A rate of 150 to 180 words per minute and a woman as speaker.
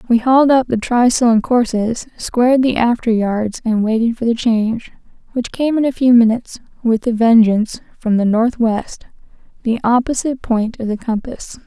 Yes: average, 175 wpm; female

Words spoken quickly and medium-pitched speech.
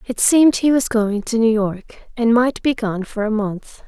No: fast, 230 wpm; high, 225 Hz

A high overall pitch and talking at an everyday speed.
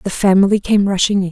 No: high, 195 Hz; fast, 230 wpm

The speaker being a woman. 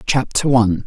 No: male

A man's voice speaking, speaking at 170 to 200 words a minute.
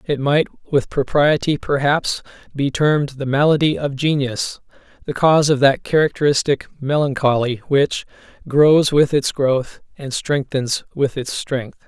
No: male; slow, 135 wpm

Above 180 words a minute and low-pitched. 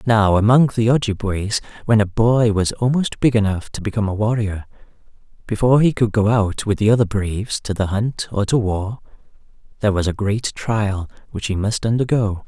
Yes: average, 190 wpm; low, 110 Hz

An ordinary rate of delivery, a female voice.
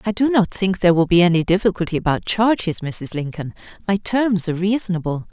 Yes: average, 190 wpm; female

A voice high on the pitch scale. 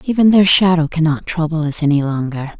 No: medium, 160 Hz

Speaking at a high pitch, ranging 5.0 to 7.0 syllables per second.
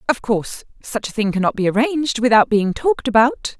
Yes: high, 235 Hz; 5.9 syllables/s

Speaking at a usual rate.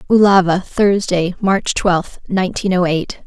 No: slow, 130 wpm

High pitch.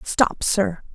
Yes: high, 215 Hz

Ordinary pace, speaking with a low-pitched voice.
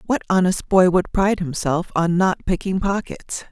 No: average, 170 wpm; medium, 185 Hz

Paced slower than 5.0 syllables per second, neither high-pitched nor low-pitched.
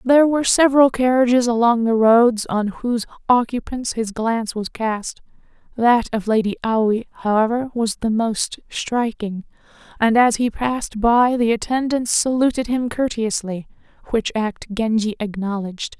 No: 4.7 syllables/s; high, 230 Hz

